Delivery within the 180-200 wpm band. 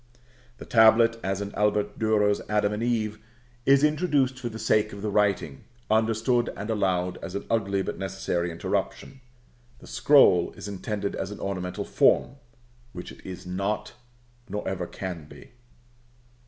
No: average, 155 wpm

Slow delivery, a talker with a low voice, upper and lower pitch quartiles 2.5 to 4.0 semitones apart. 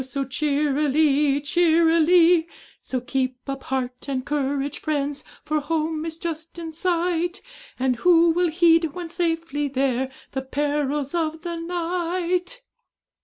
No: slow, 125 wpm; very high, 310 Hz; average, 3.4 semitones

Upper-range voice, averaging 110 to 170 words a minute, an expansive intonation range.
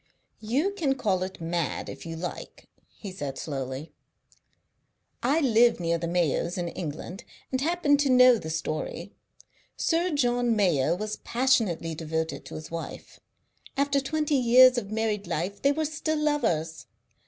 Yes: high, 215 Hz; average, 150 wpm; wide, 8.4 semitones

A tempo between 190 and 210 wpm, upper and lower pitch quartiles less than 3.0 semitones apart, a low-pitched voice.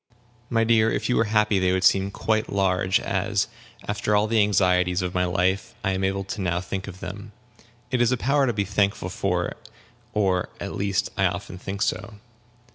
Yes: average, 195 wpm; narrow, 2.4 semitones; low, 100 Hz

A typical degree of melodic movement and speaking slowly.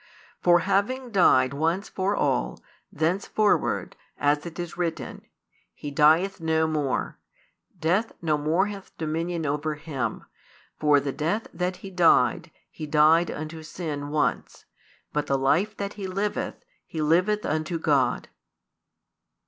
Yes: average, 3.8 semitones; slow, 130 wpm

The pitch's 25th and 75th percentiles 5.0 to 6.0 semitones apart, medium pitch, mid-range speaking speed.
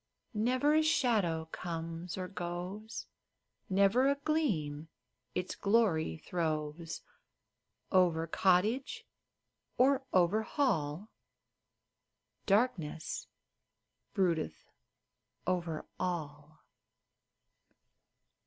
No: average, 5.3 semitones; medium, 180 Hz; slow, 70 wpm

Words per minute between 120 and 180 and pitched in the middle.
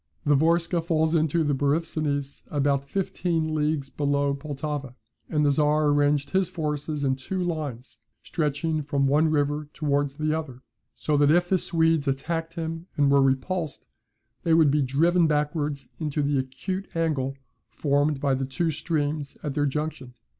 Yes: average, 160 wpm; medium, 150 Hz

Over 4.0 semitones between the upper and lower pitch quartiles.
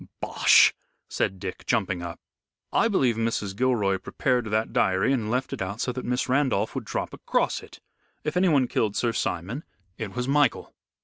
Yes: average, 4.7 semitones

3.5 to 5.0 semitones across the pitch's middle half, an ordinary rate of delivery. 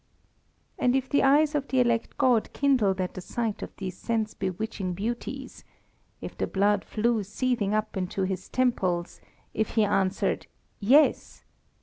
Yes: average, 4.6 semitones; average, 150 wpm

